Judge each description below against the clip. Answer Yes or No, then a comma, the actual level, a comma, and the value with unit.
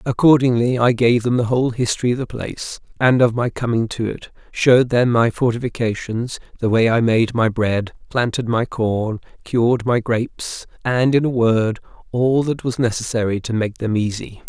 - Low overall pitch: Yes, low, 120 Hz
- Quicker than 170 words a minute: Yes, average, 180 wpm